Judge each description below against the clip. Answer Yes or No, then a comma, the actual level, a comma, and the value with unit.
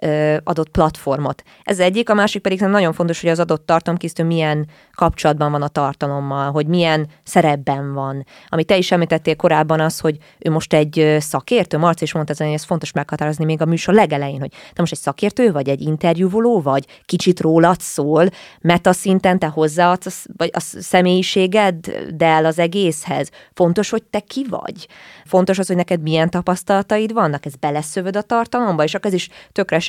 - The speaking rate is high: Yes, fast, 175 wpm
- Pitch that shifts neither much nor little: Yes, average, 3.5 semitones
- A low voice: No, medium, 165 Hz